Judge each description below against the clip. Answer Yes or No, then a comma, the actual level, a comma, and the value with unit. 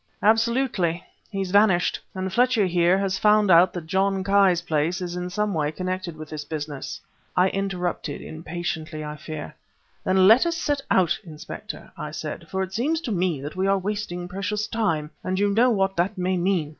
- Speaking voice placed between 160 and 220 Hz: Yes, medium, 185 Hz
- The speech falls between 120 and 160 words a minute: No, average, 185 wpm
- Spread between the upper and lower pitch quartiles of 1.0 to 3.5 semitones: Yes, average, 2.9 semitones